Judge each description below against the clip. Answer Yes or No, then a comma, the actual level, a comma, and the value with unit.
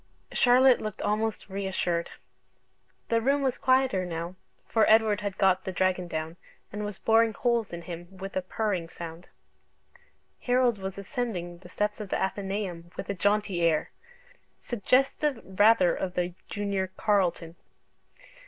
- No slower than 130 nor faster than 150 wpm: Yes, average, 145 wpm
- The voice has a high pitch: Yes, high, 195 Hz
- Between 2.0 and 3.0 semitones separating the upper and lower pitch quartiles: No, average, 3.7 semitones